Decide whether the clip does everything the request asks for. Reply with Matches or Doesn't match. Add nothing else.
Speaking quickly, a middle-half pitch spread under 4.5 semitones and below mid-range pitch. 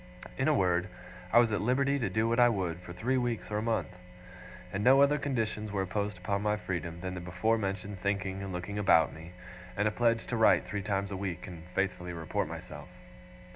Matches